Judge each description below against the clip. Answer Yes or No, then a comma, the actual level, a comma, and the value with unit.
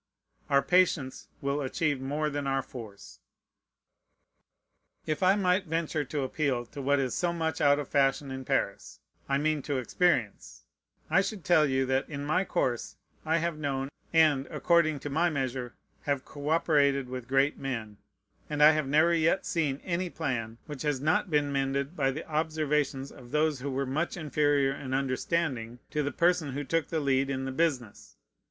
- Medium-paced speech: Yes, average, 175 wpm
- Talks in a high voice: No, medium, 145 Hz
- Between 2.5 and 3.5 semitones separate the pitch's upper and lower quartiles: Yes, average, 2.9 semitones